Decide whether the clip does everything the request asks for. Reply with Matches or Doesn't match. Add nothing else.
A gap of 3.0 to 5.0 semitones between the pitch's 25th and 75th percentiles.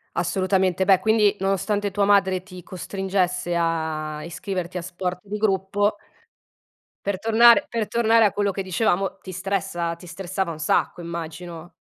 Doesn't match